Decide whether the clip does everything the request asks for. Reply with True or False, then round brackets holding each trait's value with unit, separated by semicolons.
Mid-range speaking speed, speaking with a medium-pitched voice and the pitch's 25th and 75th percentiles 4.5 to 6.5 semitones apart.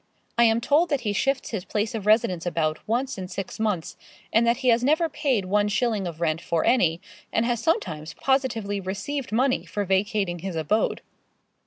False (190 wpm; 210 Hz; 4.8 semitones)